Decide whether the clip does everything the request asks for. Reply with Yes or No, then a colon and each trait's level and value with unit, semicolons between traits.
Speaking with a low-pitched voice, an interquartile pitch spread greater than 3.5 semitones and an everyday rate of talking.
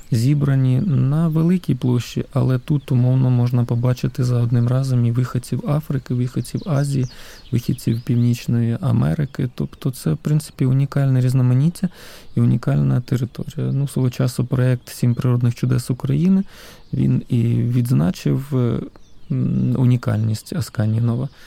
No: low, 125 Hz; narrow, 2.5 semitones; average, 120 wpm